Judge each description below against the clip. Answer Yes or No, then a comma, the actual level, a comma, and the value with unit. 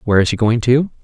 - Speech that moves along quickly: Yes, fast, 290 wpm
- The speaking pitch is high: No, low, 120 Hz